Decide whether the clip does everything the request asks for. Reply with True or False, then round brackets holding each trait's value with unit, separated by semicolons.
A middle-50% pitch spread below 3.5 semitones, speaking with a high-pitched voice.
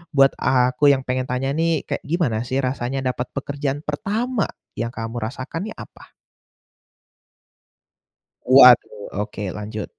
False (2.8 semitones; 130 Hz)